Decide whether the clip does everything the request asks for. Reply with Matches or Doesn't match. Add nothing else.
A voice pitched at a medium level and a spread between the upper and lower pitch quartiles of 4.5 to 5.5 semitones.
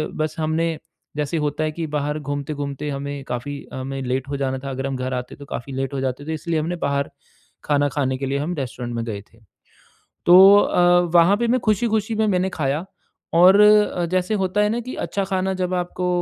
Matches